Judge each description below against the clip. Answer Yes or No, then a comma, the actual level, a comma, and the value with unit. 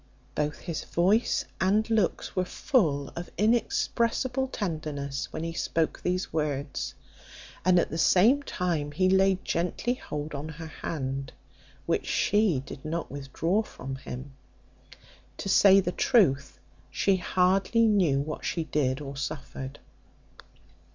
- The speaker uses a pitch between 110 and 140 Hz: No, medium, 170 Hz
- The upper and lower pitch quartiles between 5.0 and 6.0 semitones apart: Yes, wide, 5.4 semitones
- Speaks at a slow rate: Yes, slow, 130 wpm